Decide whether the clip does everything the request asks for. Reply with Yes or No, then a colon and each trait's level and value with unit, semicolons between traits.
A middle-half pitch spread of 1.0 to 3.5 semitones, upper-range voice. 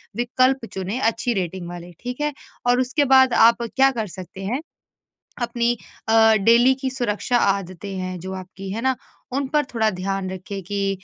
No: average, 4.7 semitones; high, 225 Hz